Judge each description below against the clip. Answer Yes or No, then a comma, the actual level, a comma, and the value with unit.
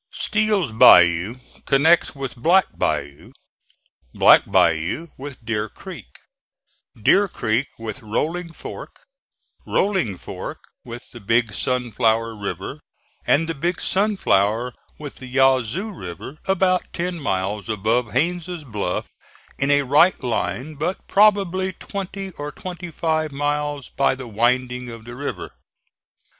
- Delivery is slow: Yes, slow, 125 wpm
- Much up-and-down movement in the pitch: Yes, wide, 7.2 semitones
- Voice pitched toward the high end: No, low, 135 Hz